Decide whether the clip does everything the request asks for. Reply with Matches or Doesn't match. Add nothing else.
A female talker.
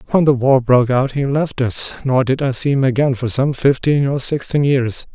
Doesn't match